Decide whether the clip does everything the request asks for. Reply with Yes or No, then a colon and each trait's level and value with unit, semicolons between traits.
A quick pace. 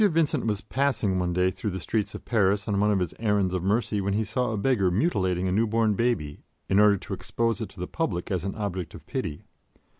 Yes: fast, 235 wpm